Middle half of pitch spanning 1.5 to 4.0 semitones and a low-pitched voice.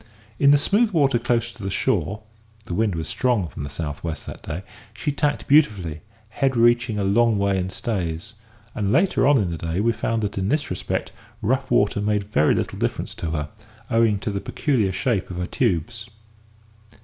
No: average, 5.0 semitones; low, 105 Hz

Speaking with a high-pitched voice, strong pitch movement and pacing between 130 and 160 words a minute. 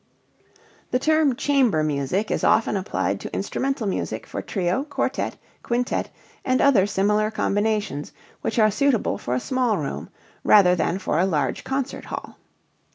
Yes: high, 215 Hz; wide, 6.0 semitones; average, 150 wpm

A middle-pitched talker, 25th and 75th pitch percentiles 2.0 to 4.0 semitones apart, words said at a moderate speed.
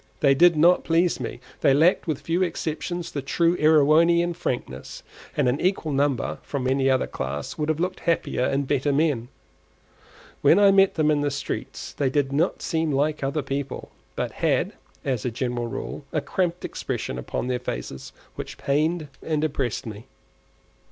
Yes: medium, 150 Hz; average, 3.6 semitones; average, 170 wpm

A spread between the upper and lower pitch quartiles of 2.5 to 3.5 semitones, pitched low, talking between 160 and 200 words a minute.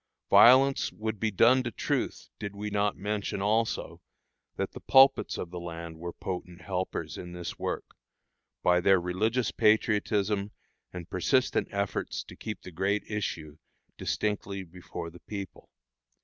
No: average, 3.2 semitones; low, 100 Hz; average, 145 wpm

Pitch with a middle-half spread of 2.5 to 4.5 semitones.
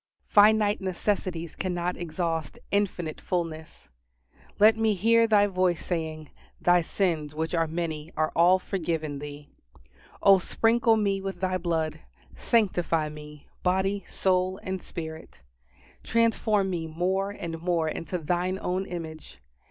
Yes: average, 3.3 semitones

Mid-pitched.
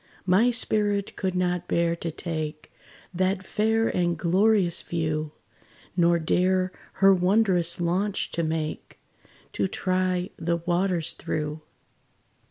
Yes: medium, 180 Hz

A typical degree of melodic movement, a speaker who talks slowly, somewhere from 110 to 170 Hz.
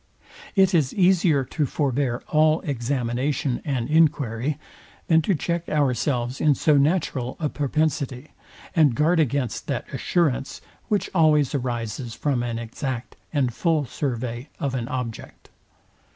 Yes: average, 3.9 semitones; slow, 130 wpm; medium, 140 Hz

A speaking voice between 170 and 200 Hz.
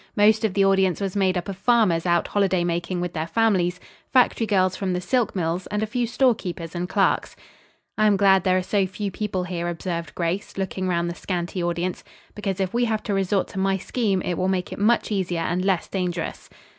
Yes: high, 190 Hz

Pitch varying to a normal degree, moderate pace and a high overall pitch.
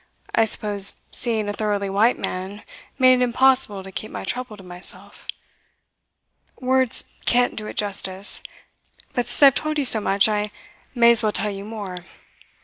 Yes: average, 3.6 semitones; average, 165 wpm; high, 215 Hz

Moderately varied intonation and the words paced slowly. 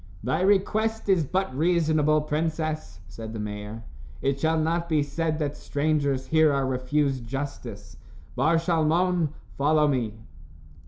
Yes: average, 3.6 semitones; slow, 130 wpm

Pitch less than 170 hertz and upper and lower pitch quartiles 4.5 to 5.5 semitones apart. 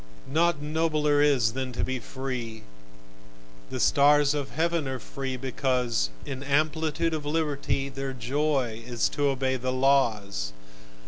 No: low, 135 Hz; narrow, 2.5 semitones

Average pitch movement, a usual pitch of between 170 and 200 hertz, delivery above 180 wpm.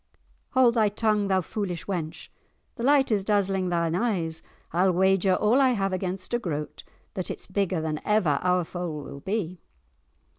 No: average, 3.4 semitones; high, 190 Hz; average, 170 wpm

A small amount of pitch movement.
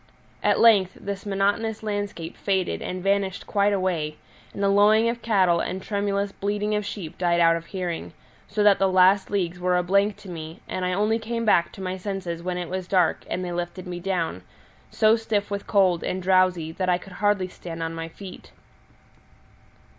Yes: narrow, 2.3 semitones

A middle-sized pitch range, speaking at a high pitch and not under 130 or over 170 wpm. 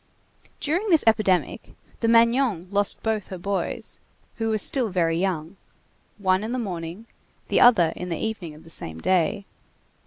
Yes: average, 4.5 semitones; high, 200 Hz; average, 160 wpm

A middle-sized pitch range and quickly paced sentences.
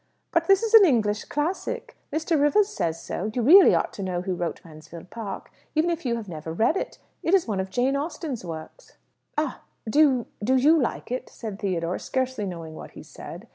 No: wide, 8.9 semitones; fast, 210 wpm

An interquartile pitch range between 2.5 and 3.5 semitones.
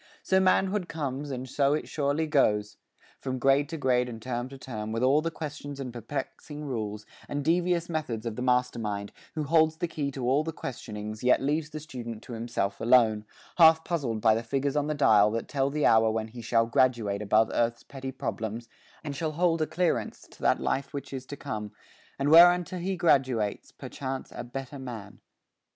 No: average, 4.8 semitones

